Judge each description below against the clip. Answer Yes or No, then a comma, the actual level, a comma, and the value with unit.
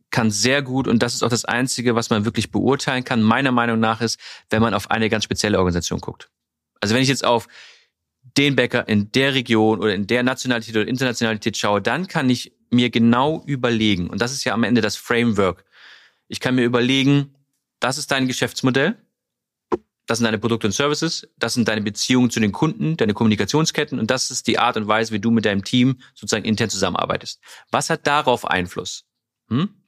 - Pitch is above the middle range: No, low, 120 Hz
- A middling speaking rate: No, fast, 200 wpm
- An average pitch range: Yes, average, 3.1 semitones